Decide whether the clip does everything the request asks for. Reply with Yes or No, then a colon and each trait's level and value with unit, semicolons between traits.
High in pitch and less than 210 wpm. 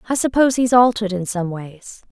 Yes: high, 215 Hz; average, 200 wpm